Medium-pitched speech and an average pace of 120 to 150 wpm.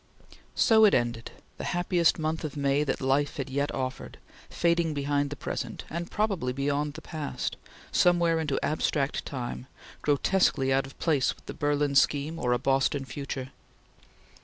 No: medium, 145 Hz; average, 160 wpm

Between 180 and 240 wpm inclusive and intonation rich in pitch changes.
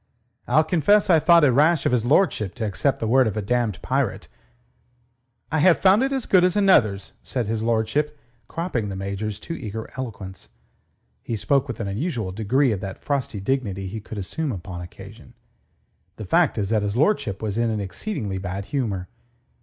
Yes: average, 185 wpm; wide, 6.6 semitones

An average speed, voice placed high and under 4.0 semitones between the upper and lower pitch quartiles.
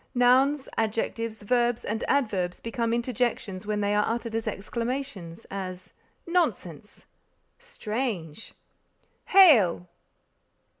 No: slow, 95 wpm; high, 225 Hz; average, 3.6 semitones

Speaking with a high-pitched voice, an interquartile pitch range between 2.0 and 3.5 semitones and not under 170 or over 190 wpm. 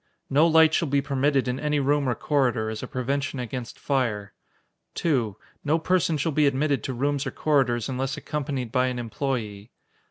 No: low, 135 Hz; average, 2.9 semitones; average, 180 wpm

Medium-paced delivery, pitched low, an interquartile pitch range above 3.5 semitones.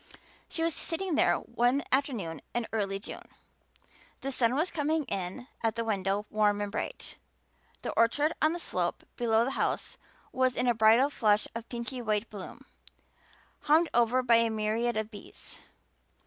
No: average, 160 wpm; high, 235 Hz; average, 4.2 semitones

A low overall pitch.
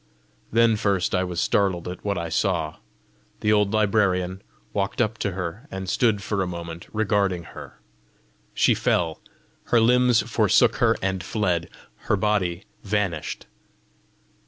Yes: very low, 95 Hz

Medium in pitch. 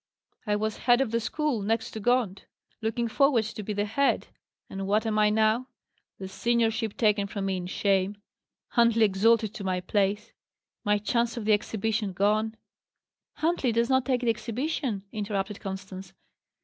No: high, 215 Hz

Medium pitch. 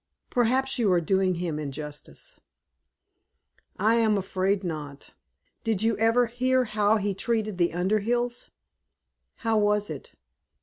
No: high, 210 Hz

